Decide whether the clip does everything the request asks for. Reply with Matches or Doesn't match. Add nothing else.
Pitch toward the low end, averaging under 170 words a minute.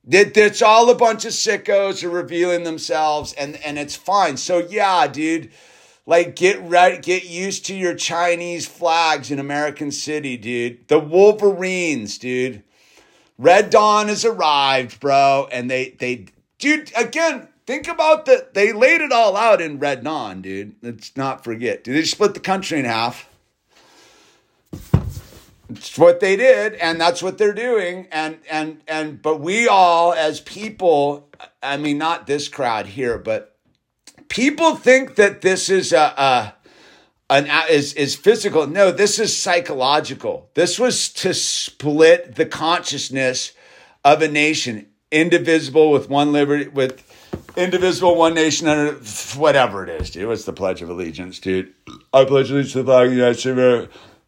Doesn't match